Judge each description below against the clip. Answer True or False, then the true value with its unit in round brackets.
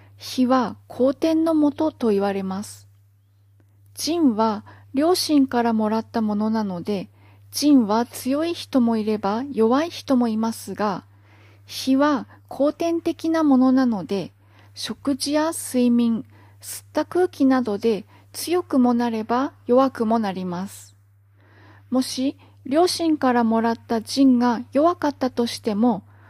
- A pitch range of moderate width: False (6.8 semitones)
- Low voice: False (235 Hz)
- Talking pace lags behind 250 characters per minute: True (235 characters per minute)